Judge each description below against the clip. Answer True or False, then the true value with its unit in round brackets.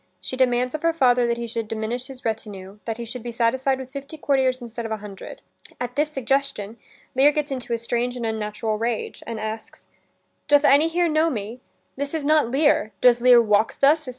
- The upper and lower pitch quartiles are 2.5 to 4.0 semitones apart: True (3.6 semitones)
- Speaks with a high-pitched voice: True (245 Hz)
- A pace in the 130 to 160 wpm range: False (205 wpm)